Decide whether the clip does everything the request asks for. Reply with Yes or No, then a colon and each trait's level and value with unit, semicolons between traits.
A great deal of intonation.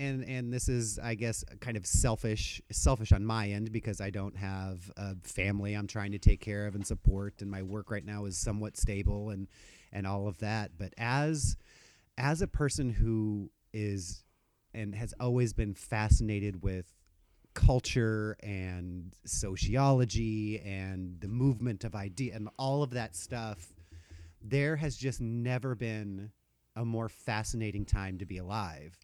No: average, 3.1 semitones